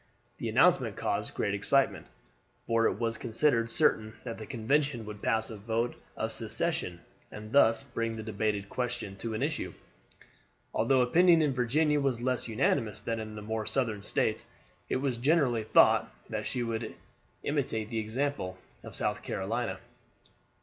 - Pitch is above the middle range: No, low, 115 Hz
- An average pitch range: Yes, average, 3.3 semitones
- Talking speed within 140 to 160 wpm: Yes, average, 155 wpm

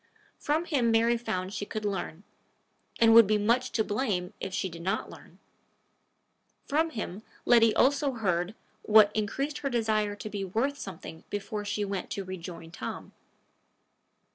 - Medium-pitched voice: No, high, 215 Hz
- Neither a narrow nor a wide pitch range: Yes, average, 3.5 semitones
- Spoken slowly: No, average, 155 wpm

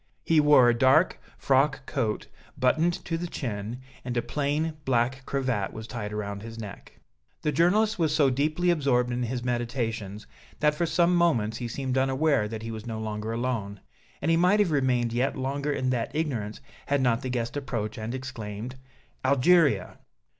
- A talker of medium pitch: No, low, 130 Hz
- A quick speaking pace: No, average, 175 wpm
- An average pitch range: Yes, average, 4.5 semitones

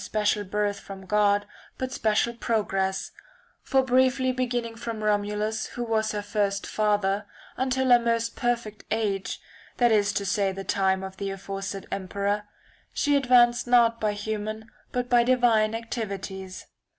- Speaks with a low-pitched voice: No, high, 215 Hz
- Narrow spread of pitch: No, average, 3.0 semitones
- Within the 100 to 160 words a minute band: Yes, average, 145 wpm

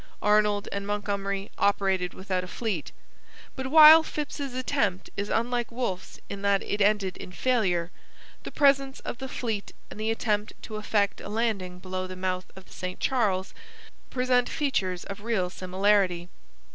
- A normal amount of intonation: Yes, average, 4.4 semitones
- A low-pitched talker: No, high, 205 Hz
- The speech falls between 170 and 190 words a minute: No, average, 160 wpm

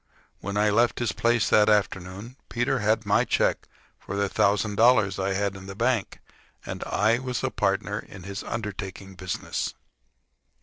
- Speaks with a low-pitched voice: Yes, low, 105 Hz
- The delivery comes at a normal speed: Yes, average, 165 wpm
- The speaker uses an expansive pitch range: No, average, 2.9 semitones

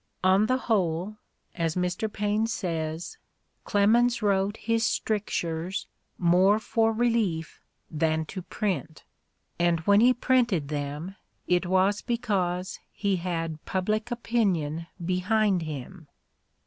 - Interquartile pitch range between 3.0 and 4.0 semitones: No, average, 4.5 semitones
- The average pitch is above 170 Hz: Yes, high, 190 Hz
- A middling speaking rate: No, slow, 115 wpm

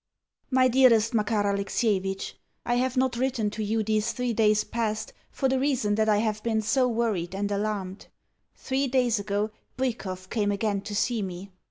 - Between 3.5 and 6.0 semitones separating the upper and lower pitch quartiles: No, average, 3.0 semitones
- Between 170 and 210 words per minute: Yes, average, 175 wpm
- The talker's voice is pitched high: Yes, high, 220 Hz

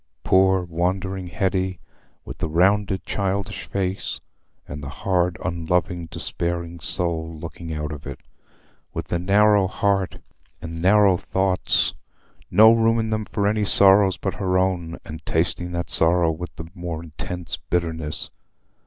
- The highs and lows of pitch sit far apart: No, average, 2.7 semitones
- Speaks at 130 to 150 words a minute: Yes, slow, 135 wpm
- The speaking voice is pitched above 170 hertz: No, very low, 90 Hz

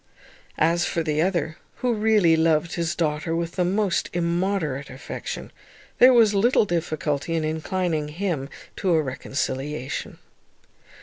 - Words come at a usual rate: No, slow, 130 wpm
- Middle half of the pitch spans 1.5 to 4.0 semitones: Yes, average, 3.5 semitones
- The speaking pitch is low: No, medium, 165 Hz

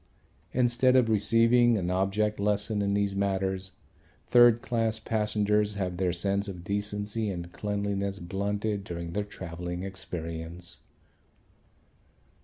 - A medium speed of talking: No, slow, 115 wpm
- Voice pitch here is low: Yes, low, 100 Hz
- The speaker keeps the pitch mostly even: Yes, narrow, 2.3 semitones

